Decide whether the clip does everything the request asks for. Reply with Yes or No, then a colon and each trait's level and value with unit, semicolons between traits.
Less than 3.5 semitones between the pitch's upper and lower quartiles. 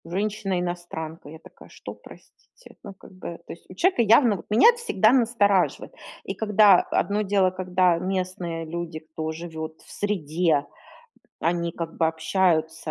No: average, 3.8 semitones